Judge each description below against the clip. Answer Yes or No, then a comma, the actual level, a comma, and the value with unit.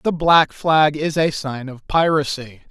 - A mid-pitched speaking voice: Yes, medium, 150 Hz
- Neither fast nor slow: Yes, average, 175 wpm